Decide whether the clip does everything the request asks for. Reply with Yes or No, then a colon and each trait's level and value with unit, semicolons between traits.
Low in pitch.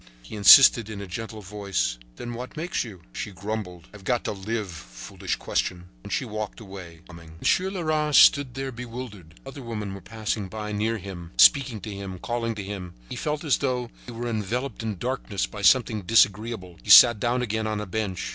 Yes: low, 110 Hz